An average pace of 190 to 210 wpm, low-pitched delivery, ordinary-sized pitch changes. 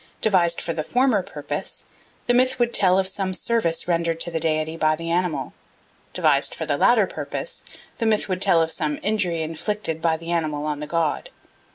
No: average, 195 wpm; medium, 170 Hz; average, 3.7 semitones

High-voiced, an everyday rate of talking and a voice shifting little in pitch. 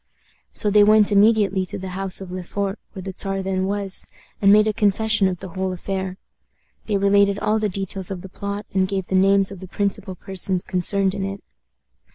No: high, 195 Hz; fast, 210 wpm; narrow, 1.3 semitones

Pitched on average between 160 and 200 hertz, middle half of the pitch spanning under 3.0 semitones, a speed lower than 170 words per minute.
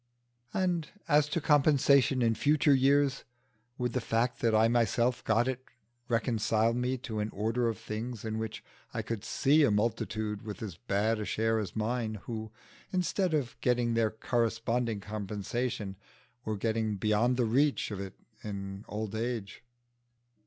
No: low, 115 Hz; narrow, 2.6 semitones; average, 155 wpm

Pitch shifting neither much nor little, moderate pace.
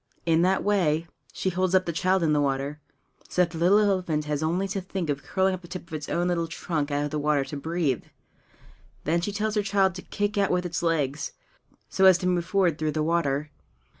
No: average, 3.6 semitones; fast, 235 wpm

